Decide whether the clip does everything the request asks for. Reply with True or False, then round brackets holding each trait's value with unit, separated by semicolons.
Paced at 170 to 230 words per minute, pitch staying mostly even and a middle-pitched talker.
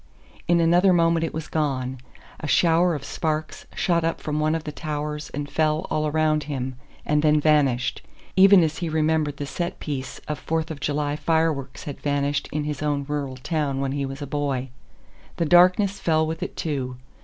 True (190 wpm; 2.1 semitones; 150 Hz)